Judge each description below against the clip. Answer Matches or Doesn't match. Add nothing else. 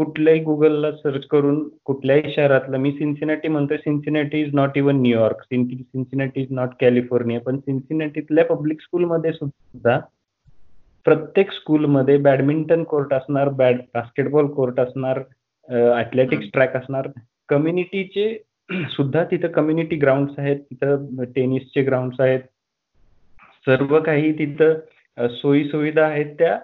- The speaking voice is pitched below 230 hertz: Matches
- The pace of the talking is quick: Doesn't match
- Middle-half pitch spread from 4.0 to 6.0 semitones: Doesn't match